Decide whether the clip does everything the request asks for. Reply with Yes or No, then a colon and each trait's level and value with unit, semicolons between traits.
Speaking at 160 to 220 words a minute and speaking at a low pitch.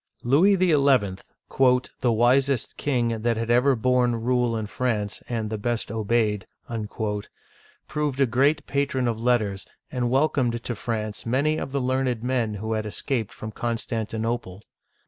No: average, 145 wpm; low, 120 Hz